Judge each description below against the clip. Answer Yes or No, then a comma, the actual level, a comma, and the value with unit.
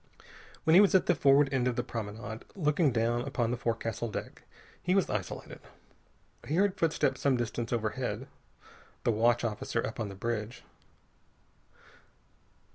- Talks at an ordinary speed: Yes, average, 150 wpm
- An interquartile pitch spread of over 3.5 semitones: Yes, average, 4.3 semitones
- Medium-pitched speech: No, low, 120 Hz